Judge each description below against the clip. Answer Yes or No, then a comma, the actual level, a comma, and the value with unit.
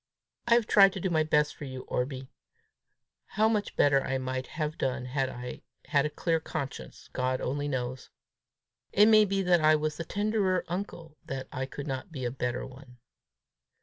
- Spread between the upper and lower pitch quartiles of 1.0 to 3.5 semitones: No, average, 5.3 semitones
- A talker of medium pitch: Yes, medium, 150 Hz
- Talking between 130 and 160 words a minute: No, average, 185 wpm